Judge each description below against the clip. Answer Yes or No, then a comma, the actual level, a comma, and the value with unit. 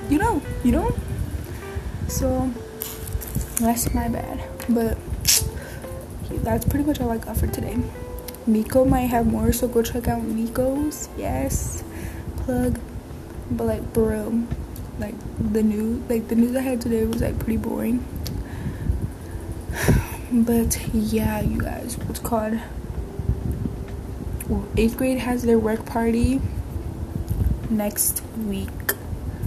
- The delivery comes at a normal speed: No, slow, 120 wpm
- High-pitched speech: Yes, high, 215 Hz